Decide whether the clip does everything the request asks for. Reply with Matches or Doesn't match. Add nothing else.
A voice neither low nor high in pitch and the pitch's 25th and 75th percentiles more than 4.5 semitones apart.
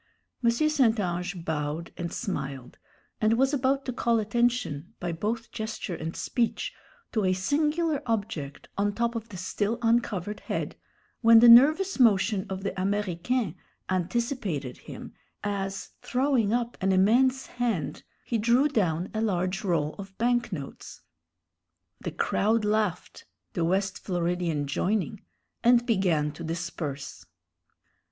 Doesn't match